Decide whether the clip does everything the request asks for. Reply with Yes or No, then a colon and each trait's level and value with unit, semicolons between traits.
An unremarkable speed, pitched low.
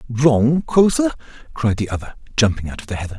Yes: average, 190 wpm; low, 110 Hz